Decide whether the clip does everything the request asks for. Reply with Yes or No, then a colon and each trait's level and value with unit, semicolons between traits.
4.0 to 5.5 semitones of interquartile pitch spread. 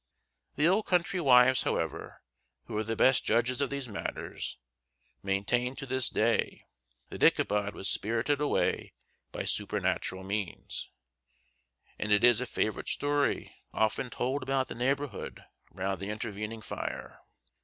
Yes: average, 4.3 semitones